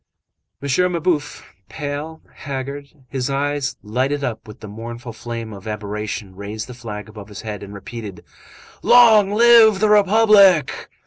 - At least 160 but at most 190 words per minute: No, average, 140 wpm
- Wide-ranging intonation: Yes, wide, 7.2 semitones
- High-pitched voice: No, low, 130 Hz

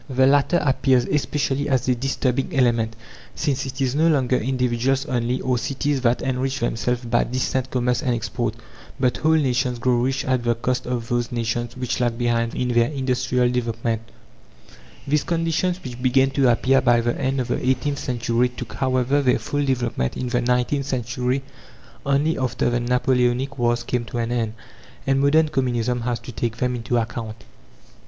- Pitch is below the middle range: Yes, low, 125 Hz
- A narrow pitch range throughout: Yes, narrow, 2.0 semitones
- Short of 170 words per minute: No, average, 175 wpm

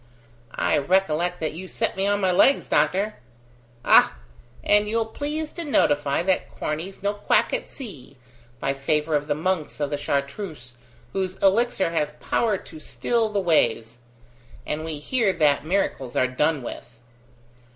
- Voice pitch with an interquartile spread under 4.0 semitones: No, wide, 5.6 semitones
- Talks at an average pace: Yes, average, 155 wpm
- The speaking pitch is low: No, medium, 165 Hz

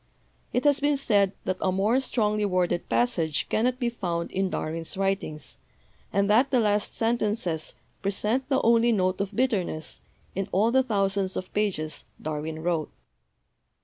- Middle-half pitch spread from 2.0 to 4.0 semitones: No, average, 4.4 semitones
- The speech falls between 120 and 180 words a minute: Yes, average, 150 wpm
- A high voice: Yes, high, 200 Hz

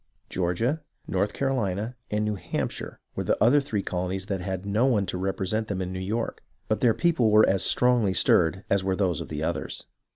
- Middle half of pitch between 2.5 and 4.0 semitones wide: Yes, average, 3.4 semitones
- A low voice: Yes, low, 100 Hz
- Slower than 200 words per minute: No, fast, 205 wpm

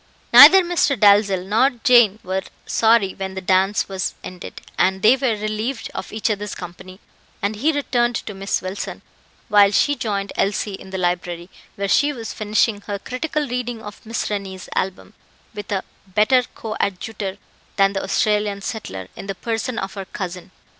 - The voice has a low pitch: No, high, 205 Hz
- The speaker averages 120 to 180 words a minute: Yes, average, 165 wpm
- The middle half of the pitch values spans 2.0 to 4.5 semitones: Yes, average, 2.9 semitones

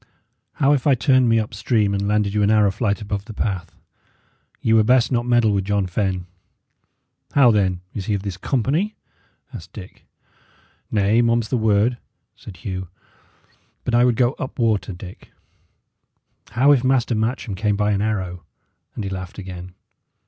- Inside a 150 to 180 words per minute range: Yes, average, 175 wpm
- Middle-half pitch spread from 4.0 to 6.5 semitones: No, average, 3.4 semitones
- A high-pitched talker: No, low, 105 Hz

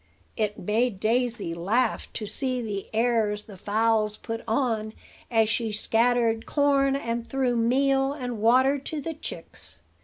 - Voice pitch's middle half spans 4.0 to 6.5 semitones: No, average, 3.0 semitones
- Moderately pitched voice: No, high, 230 Hz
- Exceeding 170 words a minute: No, average, 145 wpm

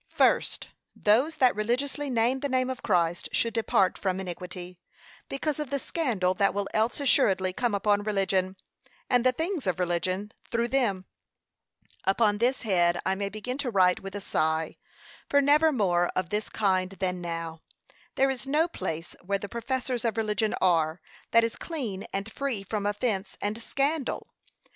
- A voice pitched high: Yes, high, 210 Hz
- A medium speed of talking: Yes, average, 170 wpm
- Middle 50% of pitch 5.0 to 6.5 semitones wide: Yes, wide, 5.4 semitones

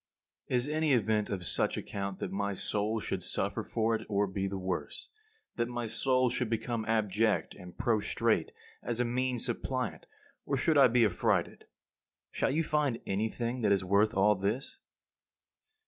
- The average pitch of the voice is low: Yes, low, 110 Hz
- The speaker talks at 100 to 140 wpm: No, average, 160 wpm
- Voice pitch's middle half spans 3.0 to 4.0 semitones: Yes, average, 3.6 semitones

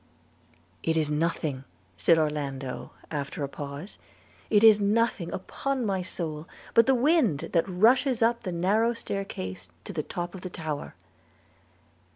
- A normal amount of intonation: No, wide, 6.7 semitones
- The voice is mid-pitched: Yes, medium, 175 Hz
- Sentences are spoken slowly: No, average, 150 wpm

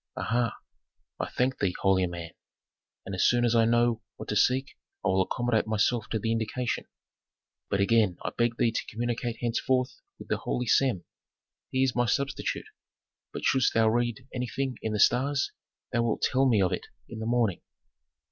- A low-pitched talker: Yes, low, 115 Hz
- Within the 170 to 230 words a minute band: Yes, average, 180 wpm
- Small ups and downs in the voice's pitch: Yes, narrow, 2.3 semitones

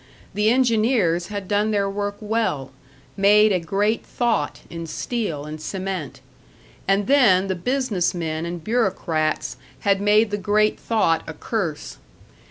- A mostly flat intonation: No, average, 4.1 semitones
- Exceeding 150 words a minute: No, average, 140 wpm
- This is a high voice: Yes, high, 200 Hz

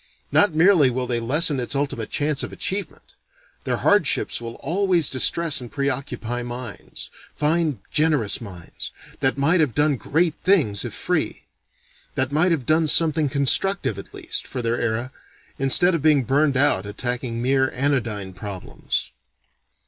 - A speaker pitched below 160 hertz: Yes, low, 135 Hz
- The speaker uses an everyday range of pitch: Yes, average, 4.6 semitones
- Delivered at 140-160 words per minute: Yes, average, 150 wpm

